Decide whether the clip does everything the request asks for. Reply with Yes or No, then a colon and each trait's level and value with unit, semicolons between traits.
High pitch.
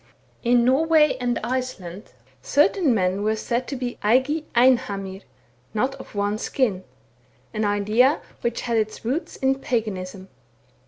Yes: high, 235 Hz